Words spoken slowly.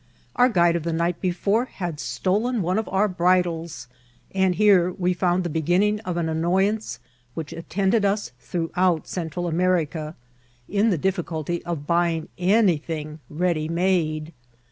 No: average, 145 wpm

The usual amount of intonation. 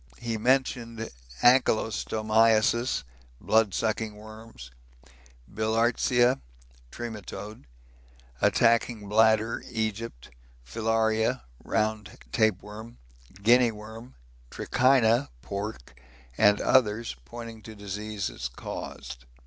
No: narrow, 1.6 semitones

